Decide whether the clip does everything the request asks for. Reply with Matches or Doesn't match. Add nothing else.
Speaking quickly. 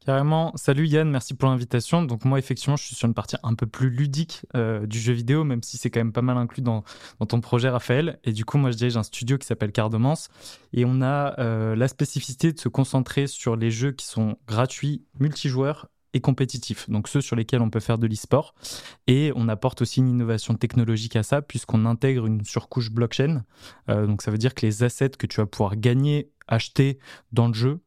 Matches